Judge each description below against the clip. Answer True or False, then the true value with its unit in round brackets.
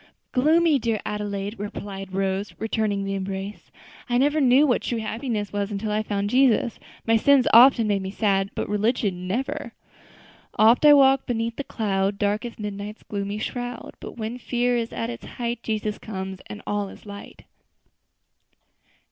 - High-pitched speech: True (215 Hz)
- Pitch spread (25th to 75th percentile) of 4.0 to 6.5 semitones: False (3.2 semitones)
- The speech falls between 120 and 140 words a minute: False (165 wpm)